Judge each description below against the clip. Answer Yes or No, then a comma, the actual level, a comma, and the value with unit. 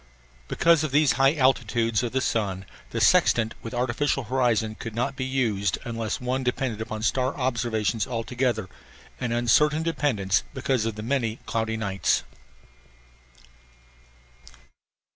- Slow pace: Yes, slow, 130 wpm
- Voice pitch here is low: Yes, low, 120 Hz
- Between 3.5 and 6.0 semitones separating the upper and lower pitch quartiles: No, average, 3.1 semitones